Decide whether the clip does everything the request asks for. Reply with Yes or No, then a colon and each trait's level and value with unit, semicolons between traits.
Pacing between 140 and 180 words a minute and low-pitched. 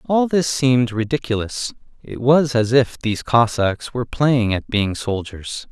Yes: average, 155 wpm; low, 120 Hz